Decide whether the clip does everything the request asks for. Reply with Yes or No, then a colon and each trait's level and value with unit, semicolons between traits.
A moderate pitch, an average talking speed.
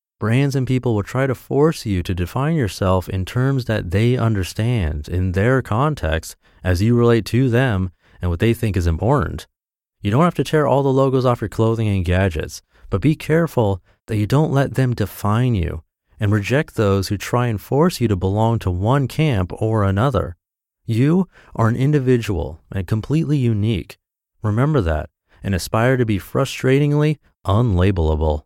No: low, 110 Hz; average, 175 wpm